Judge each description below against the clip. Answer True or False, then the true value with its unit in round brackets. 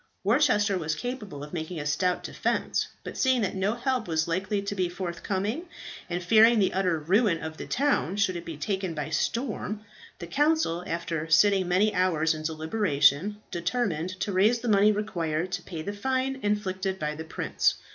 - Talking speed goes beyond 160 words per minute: True (180 wpm)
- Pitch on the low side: False (190 Hz)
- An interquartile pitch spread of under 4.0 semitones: False (4.3 semitones)